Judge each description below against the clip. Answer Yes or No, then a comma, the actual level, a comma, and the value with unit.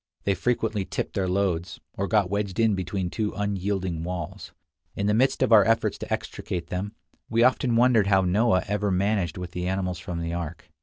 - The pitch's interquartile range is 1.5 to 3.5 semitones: Yes, average, 2.8 semitones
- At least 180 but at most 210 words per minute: Yes, average, 195 wpm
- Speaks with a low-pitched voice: Yes, low, 100 Hz